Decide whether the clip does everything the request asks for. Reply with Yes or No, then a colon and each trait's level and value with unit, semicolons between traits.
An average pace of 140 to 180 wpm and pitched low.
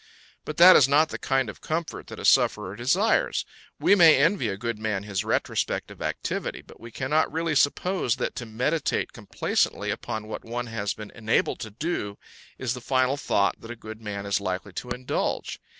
No: average, 195 wpm; low, 120 Hz